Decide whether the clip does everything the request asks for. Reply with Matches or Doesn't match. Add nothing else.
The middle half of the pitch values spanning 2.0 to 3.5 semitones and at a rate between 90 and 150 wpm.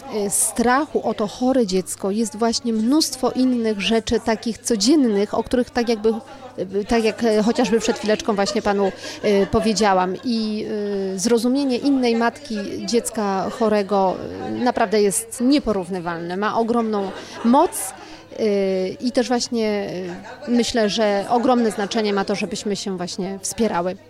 Matches